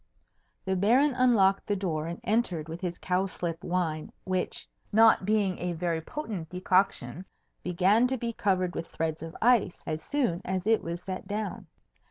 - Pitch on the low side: No, medium, 185 Hz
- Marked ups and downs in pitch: No, average, 3.9 semitones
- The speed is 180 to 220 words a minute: No, average, 165 wpm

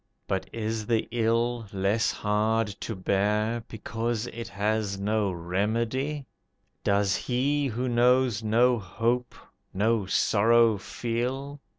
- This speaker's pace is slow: Yes, slow, 110 wpm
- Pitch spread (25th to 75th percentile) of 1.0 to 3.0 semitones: Yes, narrow, 2.5 semitones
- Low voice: Yes, low, 115 Hz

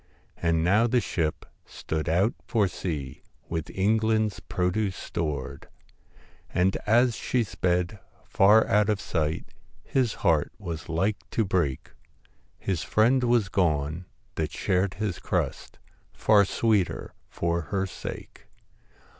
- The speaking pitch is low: Yes, very low, 95 Hz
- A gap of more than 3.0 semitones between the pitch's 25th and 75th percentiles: Yes, average, 4.5 semitones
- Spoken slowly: Yes, slow, 120 wpm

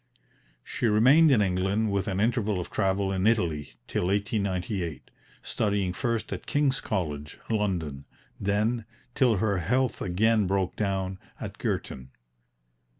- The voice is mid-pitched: No, low, 100 Hz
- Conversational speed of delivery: No, slow, 130 wpm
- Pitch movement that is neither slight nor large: Yes, average, 3.2 semitones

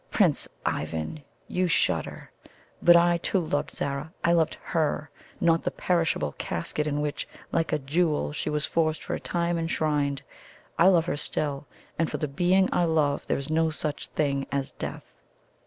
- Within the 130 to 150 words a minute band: No, average, 170 wpm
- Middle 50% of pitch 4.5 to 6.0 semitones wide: No, average, 2.8 semitones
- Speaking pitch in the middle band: Yes, medium, 155 Hz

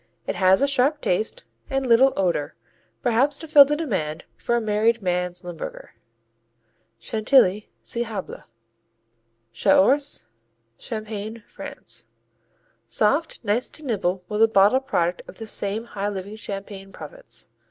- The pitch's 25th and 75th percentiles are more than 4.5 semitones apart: Yes, wide, 5.4 semitones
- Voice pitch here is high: Yes, high, 215 Hz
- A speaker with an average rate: No, slow, 130 wpm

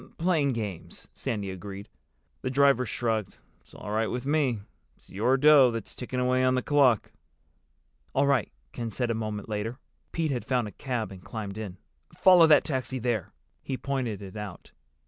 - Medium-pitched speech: No, low, 120 Hz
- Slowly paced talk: No, average, 175 wpm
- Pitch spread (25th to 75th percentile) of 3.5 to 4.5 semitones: Yes, average, 4.1 semitones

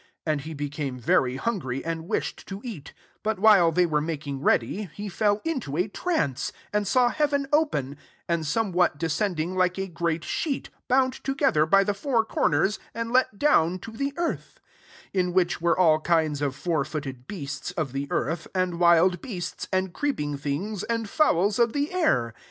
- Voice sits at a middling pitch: Yes, medium, 180 Hz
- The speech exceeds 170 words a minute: Yes, average, 185 wpm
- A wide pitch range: Yes, wide, 6.3 semitones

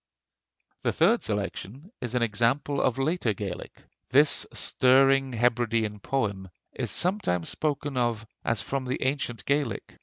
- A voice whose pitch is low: Yes, low, 125 Hz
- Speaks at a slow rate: Yes, slow, 130 wpm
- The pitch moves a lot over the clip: No, average, 4.0 semitones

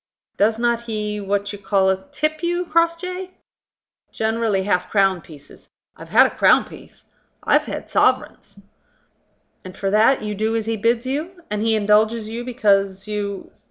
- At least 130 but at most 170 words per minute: Yes, average, 160 wpm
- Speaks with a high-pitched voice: Yes, high, 215 Hz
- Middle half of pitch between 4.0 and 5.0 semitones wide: No, average, 3.2 semitones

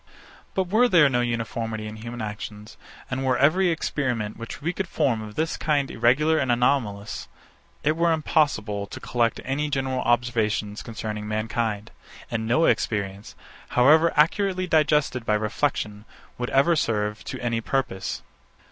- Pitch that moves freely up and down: Yes, wide, 5.7 semitones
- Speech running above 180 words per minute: No, average, 145 wpm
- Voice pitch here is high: No, low, 120 Hz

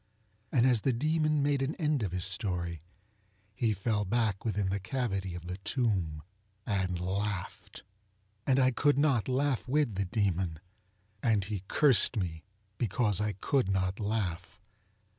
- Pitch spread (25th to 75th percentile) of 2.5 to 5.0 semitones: No, wide, 5.5 semitones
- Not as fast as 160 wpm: Yes, average, 150 wpm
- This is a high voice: No, low, 105 Hz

